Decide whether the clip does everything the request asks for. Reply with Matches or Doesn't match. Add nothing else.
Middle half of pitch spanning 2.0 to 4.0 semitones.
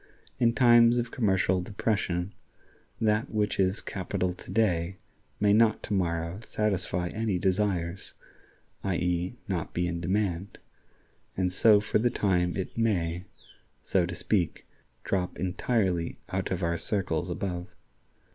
Matches